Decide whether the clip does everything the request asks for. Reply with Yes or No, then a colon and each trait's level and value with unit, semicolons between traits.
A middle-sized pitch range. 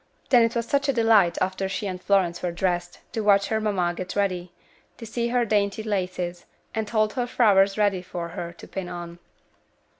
Yes: average, 3.6 semitones